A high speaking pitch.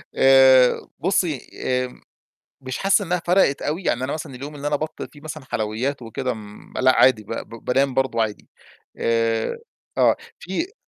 No: low, 135 Hz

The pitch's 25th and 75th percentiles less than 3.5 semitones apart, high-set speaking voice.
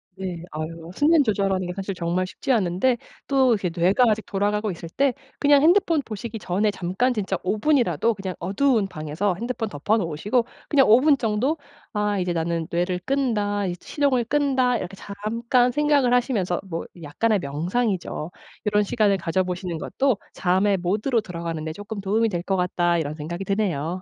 No: average, 5.1 semitones; high, 200 Hz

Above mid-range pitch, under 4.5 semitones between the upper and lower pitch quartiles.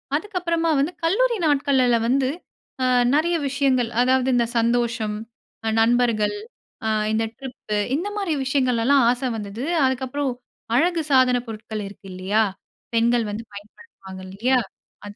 Yes: very high, 250 Hz; average, 4.0 semitones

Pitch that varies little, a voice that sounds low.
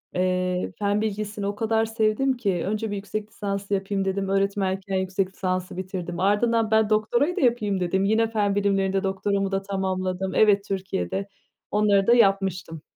No: narrow, 1.9 semitones; high, 200 Hz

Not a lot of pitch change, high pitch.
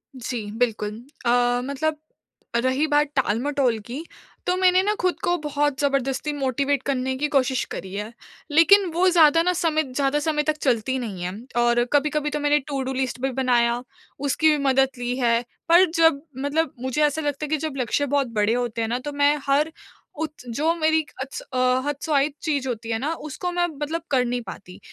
No: average, 3.6 semitones; very high, 280 Hz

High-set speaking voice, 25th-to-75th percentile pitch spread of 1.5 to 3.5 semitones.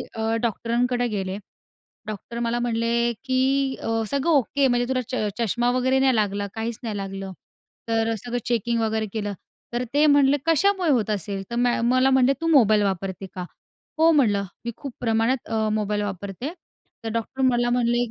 Yes: high, 235 Hz; average, 3.2 semitones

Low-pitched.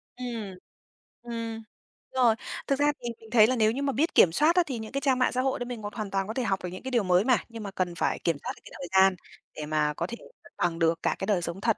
No: high, 220 Hz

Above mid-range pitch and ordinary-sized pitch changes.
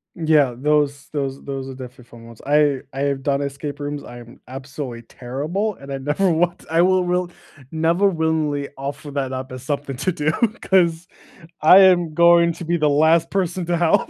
No: medium, 150 Hz; average, 3.9 semitones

